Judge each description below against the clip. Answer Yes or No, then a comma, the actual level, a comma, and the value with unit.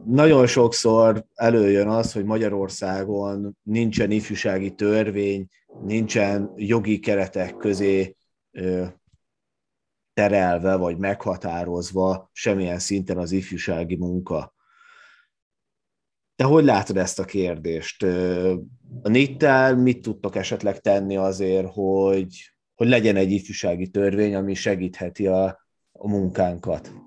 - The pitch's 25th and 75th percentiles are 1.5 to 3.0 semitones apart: Yes, narrow, 2.4 semitones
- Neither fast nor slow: No, slow, 100 wpm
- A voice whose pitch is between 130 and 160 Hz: No, low, 100 Hz